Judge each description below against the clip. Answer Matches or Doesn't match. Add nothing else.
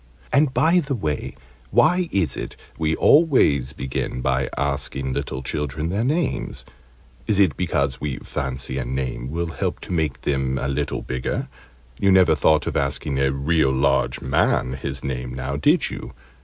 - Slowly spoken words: Doesn't match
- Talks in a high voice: Doesn't match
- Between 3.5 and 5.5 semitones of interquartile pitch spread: Matches